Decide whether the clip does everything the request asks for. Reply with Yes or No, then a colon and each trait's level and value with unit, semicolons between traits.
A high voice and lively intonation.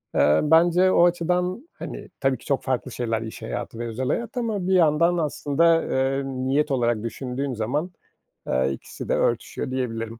No: low, 135 Hz; wide, 6.3 semitones